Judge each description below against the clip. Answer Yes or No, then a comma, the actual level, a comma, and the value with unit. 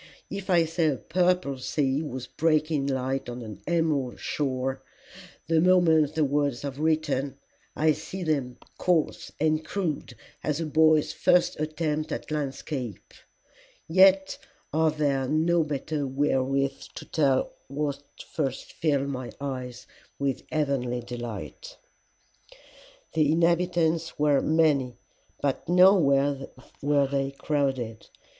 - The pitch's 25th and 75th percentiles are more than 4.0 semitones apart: No, average, 2.9 semitones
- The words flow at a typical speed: No, slow, 125 wpm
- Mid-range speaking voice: Yes, medium, 150 Hz